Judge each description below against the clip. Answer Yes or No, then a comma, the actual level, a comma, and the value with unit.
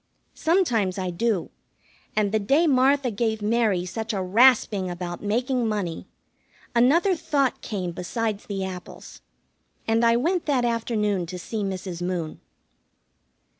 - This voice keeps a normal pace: No, slow, 130 wpm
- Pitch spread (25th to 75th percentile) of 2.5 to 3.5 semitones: No, average, 4.8 semitones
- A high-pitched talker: Yes, high, 220 Hz